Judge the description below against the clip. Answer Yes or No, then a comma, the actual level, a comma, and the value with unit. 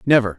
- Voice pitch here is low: Yes, low, 115 Hz